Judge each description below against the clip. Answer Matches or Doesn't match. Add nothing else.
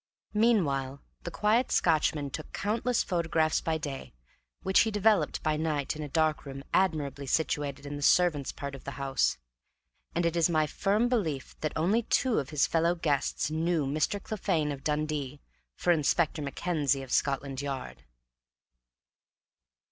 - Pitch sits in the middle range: Matches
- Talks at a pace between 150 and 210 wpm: Matches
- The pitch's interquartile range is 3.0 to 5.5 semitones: Matches